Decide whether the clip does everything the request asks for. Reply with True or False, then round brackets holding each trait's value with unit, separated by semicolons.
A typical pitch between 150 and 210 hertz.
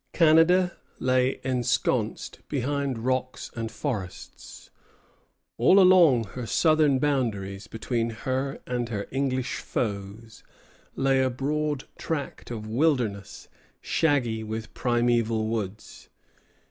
False (125 Hz)